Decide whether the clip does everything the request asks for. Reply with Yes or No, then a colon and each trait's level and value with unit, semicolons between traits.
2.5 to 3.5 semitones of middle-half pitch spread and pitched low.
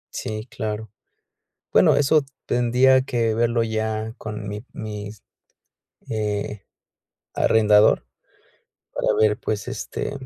No: narrow, 1.8 semitones; low, 110 Hz